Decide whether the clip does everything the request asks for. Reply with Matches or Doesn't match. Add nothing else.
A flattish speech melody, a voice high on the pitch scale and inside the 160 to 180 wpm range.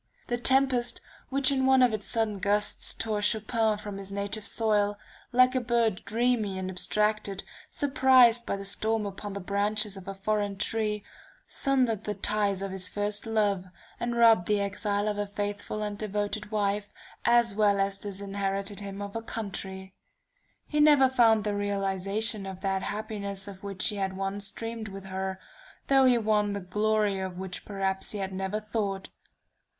Matches